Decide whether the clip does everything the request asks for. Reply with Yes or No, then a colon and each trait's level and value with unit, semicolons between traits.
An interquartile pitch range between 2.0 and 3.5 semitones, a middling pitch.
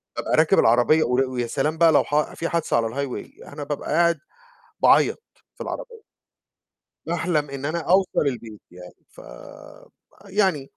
No: average, 4.7 semitones; medium, 150 Hz